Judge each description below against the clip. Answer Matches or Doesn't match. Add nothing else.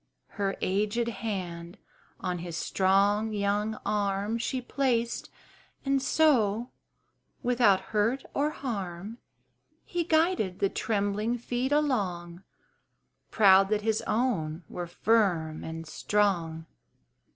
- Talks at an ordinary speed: Doesn't match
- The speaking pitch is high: Matches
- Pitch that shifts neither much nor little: Matches